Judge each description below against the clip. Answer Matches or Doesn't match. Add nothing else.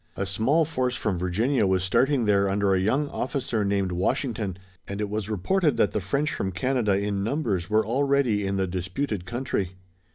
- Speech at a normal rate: Matches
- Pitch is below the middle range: Matches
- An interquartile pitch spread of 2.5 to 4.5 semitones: Doesn't match